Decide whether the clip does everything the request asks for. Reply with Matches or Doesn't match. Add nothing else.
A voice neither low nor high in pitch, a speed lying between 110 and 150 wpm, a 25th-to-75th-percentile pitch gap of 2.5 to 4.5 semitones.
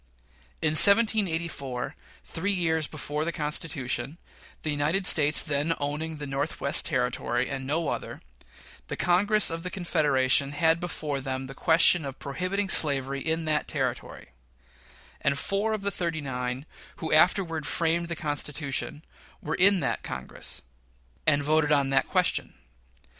Matches